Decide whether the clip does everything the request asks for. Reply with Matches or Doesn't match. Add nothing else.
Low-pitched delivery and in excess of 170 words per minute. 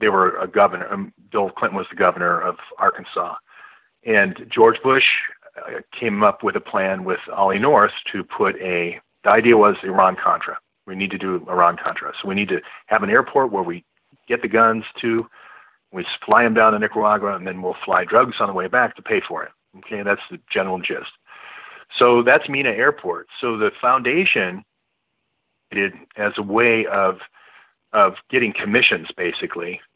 Matches